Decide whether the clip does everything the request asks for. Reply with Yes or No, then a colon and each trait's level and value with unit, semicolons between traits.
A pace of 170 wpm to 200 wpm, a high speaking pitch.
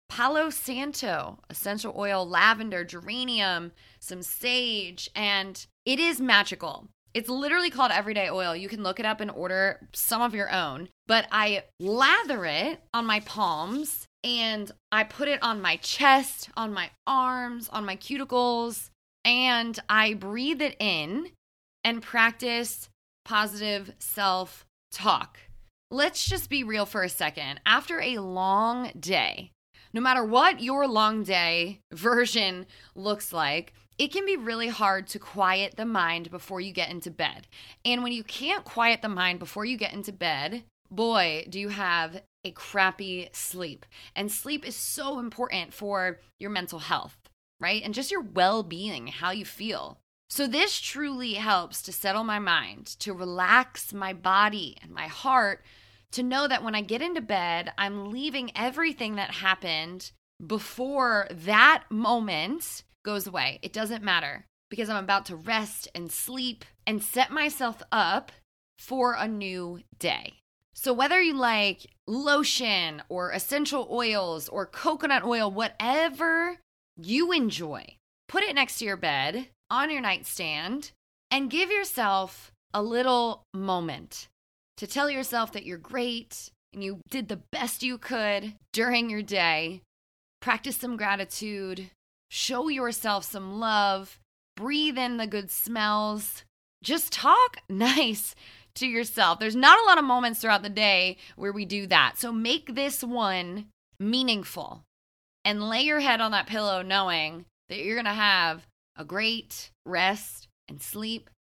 No: average, 150 wpm; high, 215 Hz